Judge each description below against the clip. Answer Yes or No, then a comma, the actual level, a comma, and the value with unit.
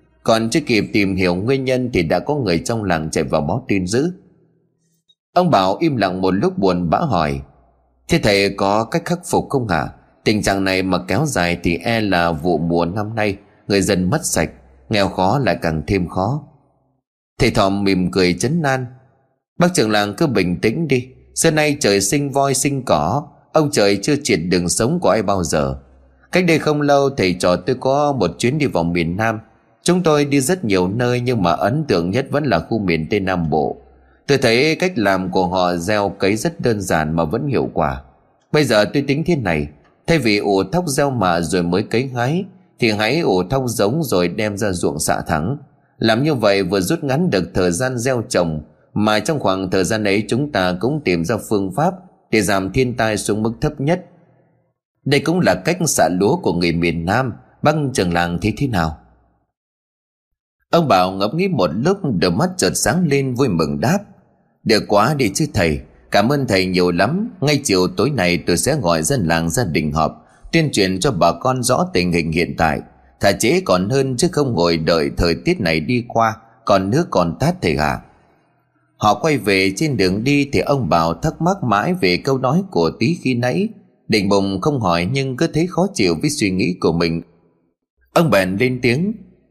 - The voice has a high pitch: No, low, 110 Hz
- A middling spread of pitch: No, wide, 7.9 semitones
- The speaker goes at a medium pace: Yes, average, 210 wpm